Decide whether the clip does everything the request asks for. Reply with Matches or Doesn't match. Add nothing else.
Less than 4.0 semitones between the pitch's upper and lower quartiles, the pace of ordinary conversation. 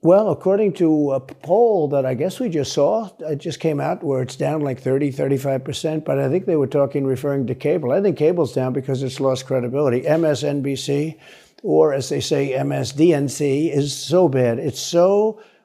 Matches